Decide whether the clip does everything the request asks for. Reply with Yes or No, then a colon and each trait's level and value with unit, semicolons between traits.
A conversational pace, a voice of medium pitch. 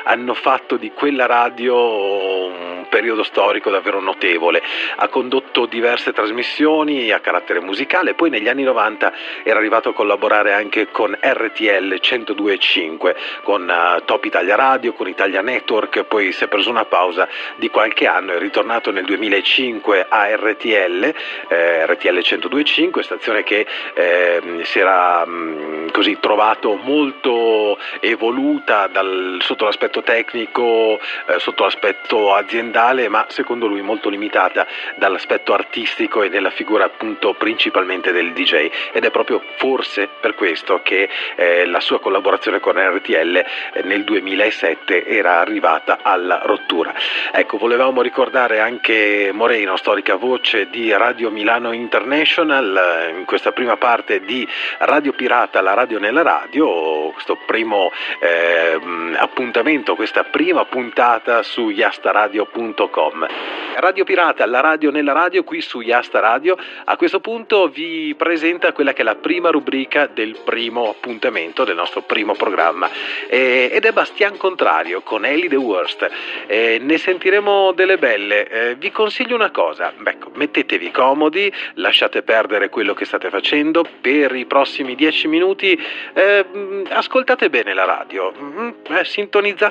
Yes: average, 140 wpm; medium, 155 Hz